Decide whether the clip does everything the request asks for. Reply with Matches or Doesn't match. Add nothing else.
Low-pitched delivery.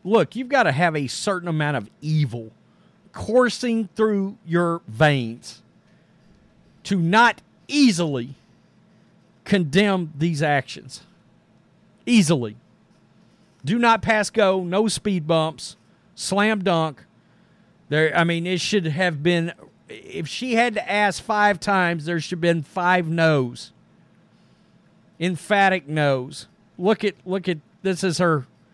Doesn't match